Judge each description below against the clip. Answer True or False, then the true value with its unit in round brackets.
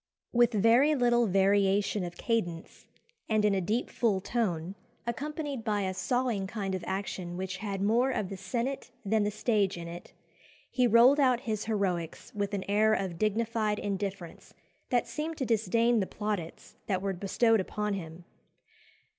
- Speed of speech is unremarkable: True (165 wpm)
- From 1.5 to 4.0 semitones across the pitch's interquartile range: True (3.5 semitones)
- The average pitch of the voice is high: True (210 Hz)